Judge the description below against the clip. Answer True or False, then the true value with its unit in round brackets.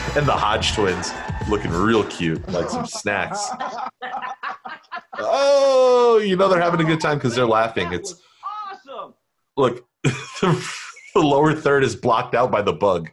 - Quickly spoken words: False (150 wpm)